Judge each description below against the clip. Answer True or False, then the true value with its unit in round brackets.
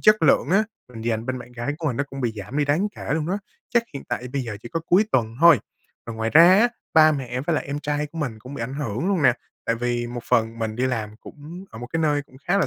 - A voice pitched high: False (135 Hz)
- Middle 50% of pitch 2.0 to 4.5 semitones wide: False (5.1 semitones)